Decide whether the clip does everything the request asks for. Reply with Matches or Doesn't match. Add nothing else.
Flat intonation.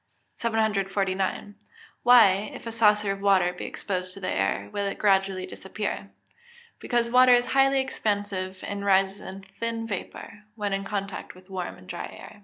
Matches